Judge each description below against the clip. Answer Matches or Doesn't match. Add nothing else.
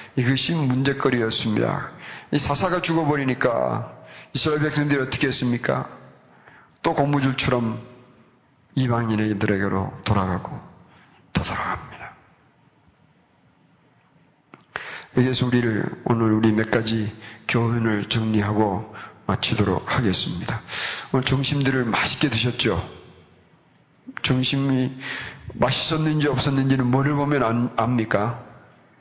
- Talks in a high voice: Doesn't match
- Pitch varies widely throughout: Doesn't match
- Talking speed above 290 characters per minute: Doesn't match